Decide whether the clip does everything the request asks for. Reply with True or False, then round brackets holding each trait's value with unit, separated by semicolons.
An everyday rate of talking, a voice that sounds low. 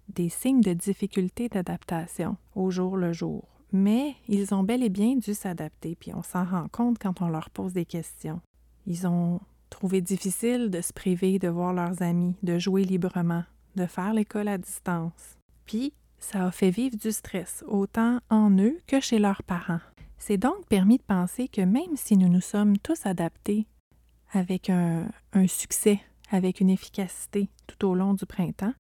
False (180 wpm; 190 Hz)